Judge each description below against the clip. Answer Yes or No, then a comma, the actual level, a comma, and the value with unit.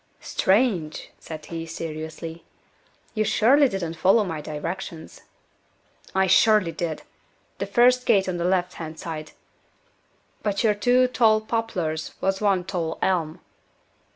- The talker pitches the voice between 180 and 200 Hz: Yes, medium, 185 Hz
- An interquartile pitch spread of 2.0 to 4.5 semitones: No, average, 4.9 semitones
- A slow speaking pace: Yes, slow, 125 wpm